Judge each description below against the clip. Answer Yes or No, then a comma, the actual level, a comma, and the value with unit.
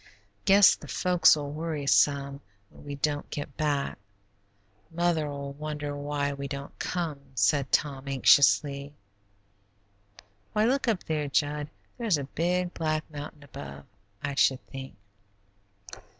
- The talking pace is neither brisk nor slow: No, slow, 120 wpm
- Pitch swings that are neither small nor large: No, narrow, 2.2 semitones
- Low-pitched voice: No, medium, 145 Hz